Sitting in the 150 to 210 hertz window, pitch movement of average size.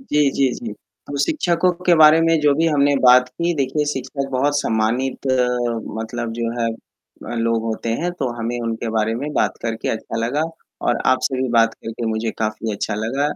No: low, 125 Hz; average, 4.3 semitones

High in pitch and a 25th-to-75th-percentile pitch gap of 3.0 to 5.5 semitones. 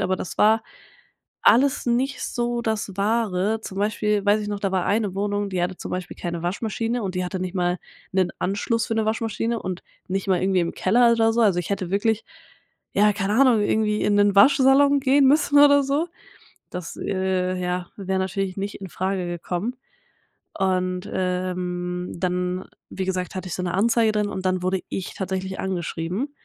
Yes: high, 195 Hz; average, 3.5 semitones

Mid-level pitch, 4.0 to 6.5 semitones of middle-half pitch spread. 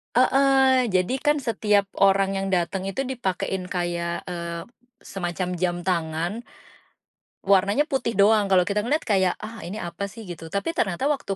No: high, 195 Hz; average, 4.5 semitones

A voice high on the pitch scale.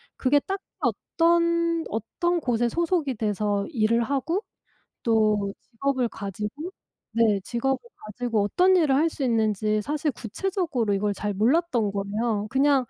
Yes: high, 240 Hz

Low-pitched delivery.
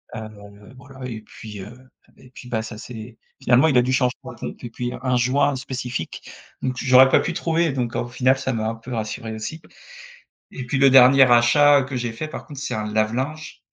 Yes: low, 125 Hz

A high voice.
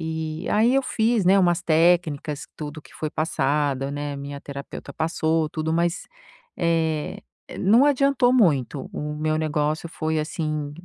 No: medium, 160 Hz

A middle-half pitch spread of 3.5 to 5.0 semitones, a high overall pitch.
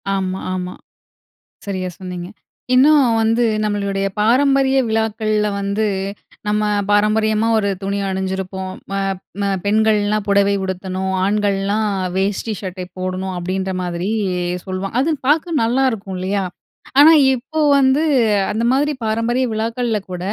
No: average, 3.1 semitones; high, 205 Hz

